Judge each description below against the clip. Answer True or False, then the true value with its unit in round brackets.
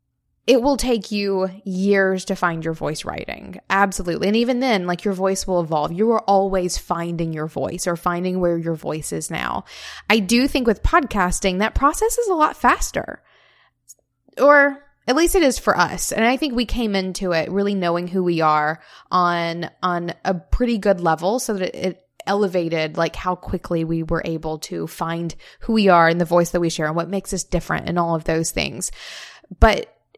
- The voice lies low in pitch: False (185 Hz)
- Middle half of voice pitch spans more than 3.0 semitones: True (4.1 semitones)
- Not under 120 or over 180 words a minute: False (200 wpm)